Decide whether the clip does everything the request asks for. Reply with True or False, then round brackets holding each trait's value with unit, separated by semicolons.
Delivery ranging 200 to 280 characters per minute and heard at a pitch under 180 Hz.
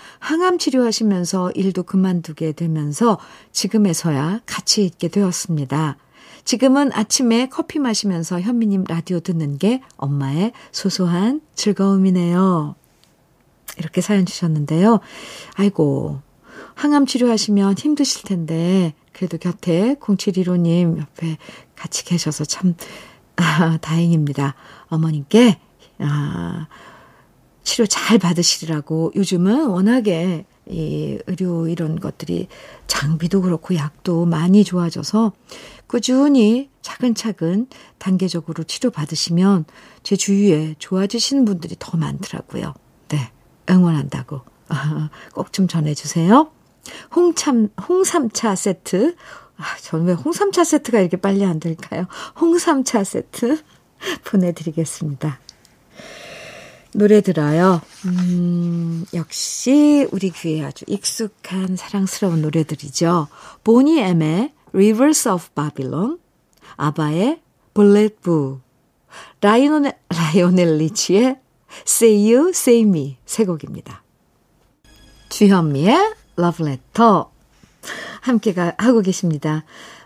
False (260 characters per minute; 185 Hz)